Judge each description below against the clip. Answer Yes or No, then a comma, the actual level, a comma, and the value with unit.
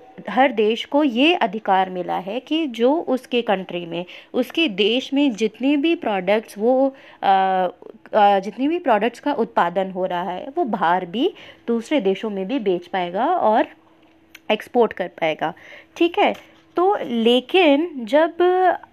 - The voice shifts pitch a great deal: Yes, wide, 7.1 semitones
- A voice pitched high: Yes, high, 235 Hz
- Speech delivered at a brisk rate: No, average, 145 wpm